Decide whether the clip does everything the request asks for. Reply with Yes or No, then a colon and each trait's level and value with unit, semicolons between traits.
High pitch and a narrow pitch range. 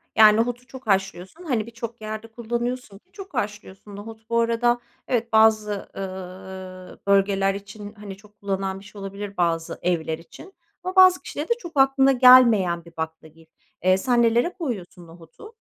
No: high, 210 Hz; average, 4.1 semitones